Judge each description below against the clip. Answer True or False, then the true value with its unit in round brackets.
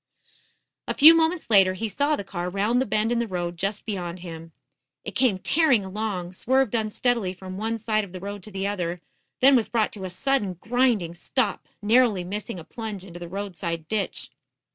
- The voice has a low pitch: False (205 Hz)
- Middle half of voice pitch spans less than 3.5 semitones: False (4.2 semitones)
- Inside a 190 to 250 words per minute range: True (195 wpm)